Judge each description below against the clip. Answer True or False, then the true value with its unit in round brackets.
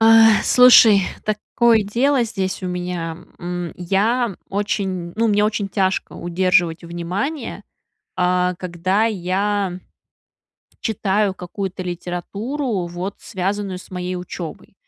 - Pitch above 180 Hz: True (190 Hz)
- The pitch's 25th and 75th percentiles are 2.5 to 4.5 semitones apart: True (2.9 semitones)